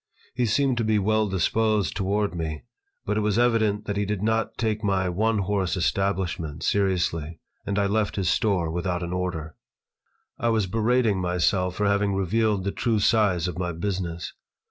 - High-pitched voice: No, low, 100 Hz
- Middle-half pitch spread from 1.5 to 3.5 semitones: Yes, average, 3.1 semitones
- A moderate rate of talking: Yes, average, 175 wpm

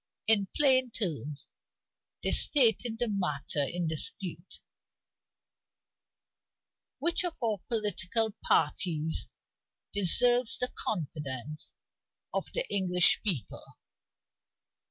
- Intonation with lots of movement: Yes, wide, 6.5 semitones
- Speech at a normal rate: No, slow, 85 wpm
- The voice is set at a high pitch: Yes, high, 200 Hz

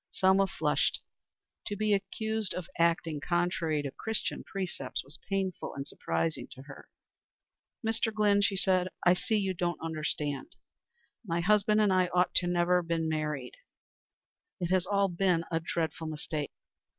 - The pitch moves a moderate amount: Yes, average, 3.5 semitones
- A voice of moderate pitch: Yes, medium, 180 Hz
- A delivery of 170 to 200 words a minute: No, average, 150 wpm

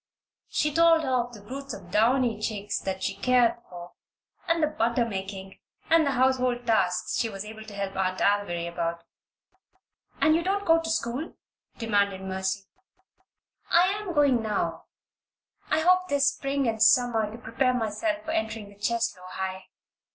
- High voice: Yes, high, 230 Hz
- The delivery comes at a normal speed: Yes, average, 165 wpm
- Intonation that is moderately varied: No, wide, 5.9 semitones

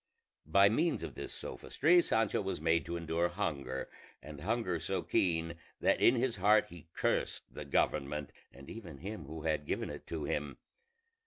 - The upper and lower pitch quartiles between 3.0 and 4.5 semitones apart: No, wide, 5.4 semitones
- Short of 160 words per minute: No, average, 170 wpm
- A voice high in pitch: No, very low, 85 Hz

